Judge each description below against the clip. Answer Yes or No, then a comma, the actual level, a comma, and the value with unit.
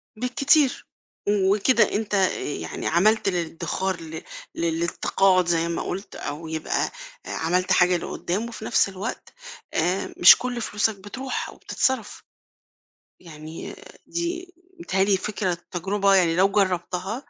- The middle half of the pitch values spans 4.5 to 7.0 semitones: No, average, 4.0 semitones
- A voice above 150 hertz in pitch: Yes, high, 190 Hz